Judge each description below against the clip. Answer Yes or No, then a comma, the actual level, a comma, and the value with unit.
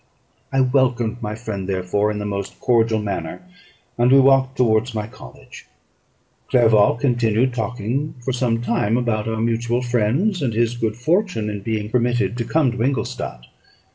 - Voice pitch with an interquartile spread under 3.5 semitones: Yes, average, 2.7 semitones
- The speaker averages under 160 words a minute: No, average, 165 wpm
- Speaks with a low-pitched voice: Yes, low, 115 Hz